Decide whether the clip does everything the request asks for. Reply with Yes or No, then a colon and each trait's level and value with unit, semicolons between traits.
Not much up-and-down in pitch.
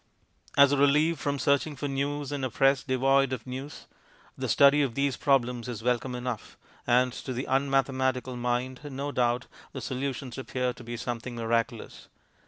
Yes: narrow, 2.2 semitones